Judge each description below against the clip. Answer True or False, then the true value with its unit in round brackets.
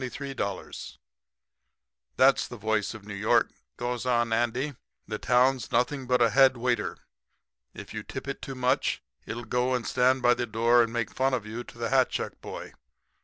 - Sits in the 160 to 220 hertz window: False (120 Hz)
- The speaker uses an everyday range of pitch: False (2.0 semitones)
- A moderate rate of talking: True (185 wpm)